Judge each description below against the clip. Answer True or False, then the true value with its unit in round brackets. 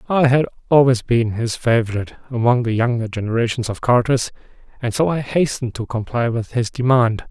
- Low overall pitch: True (120 Hz)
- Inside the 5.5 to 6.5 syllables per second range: True (5.7 syllables/s)